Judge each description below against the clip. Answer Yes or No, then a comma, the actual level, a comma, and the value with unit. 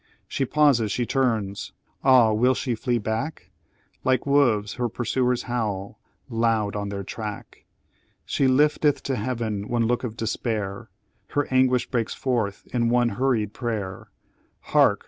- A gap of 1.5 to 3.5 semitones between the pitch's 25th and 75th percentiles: Yes, average, 3.2 semitones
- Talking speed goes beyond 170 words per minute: No, average, 140 wpm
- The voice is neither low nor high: No, low, 120 Hz